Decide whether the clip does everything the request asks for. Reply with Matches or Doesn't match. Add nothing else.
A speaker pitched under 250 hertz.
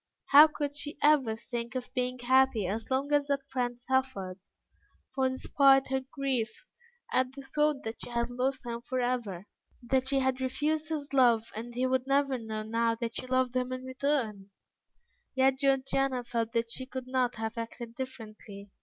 Doesn't match